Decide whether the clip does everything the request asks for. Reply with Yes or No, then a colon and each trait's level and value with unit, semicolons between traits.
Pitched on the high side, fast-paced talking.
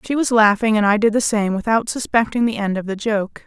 Yes: high, 215 Hz; fast, 260 wpm